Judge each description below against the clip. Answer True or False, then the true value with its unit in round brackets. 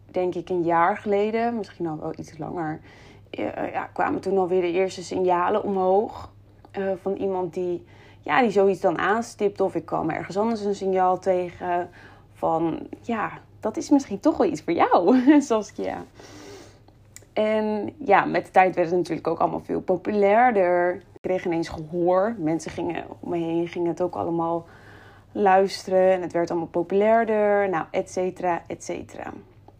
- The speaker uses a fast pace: False (165 wpm)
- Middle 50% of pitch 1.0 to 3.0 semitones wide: True (2.7 semitones)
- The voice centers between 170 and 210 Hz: True (185 Hz)